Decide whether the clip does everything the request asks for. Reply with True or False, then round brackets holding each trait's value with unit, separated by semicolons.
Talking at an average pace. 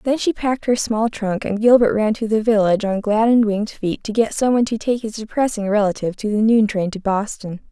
False (250 wpm)